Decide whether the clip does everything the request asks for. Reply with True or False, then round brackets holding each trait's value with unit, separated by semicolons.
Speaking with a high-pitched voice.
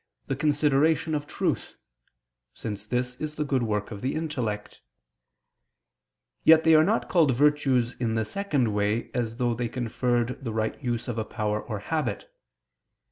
False (125 Hz)